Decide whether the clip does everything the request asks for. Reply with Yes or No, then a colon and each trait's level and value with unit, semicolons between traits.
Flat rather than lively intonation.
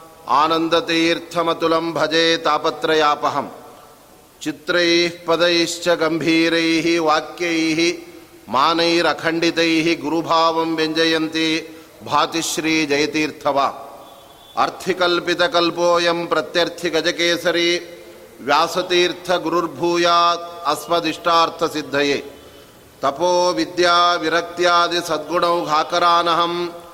Yes: narrow, 1.3 semitones